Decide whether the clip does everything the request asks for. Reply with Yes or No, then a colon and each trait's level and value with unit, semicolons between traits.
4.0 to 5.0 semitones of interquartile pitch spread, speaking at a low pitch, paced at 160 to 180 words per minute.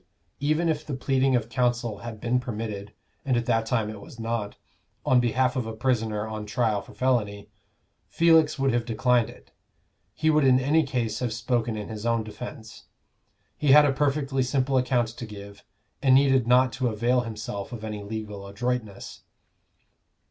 No: average, 3.2 semitones; low, 120 Hz; average, 175 wpm